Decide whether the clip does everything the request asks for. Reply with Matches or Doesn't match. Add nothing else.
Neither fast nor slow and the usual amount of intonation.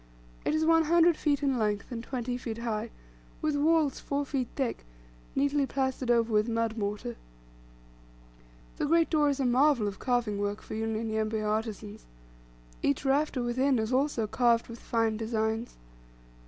Matches